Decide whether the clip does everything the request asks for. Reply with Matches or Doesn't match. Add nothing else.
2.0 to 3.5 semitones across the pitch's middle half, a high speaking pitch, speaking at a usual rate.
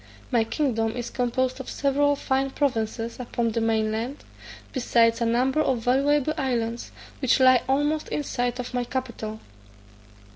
Matches